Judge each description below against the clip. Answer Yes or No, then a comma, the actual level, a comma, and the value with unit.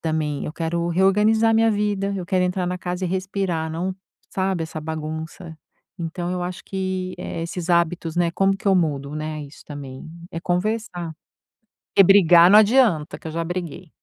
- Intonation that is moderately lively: Yes, average, 3.0 semitones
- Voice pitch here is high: No, medium, 175 Hz